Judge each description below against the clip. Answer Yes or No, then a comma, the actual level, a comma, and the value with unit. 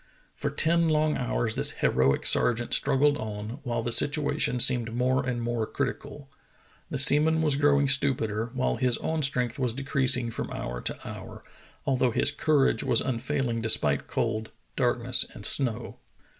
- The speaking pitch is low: Yes, low, 130 Hz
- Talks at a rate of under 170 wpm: Yes, average, 155 wpm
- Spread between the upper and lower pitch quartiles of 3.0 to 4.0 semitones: Yes, average, 3.5 semitones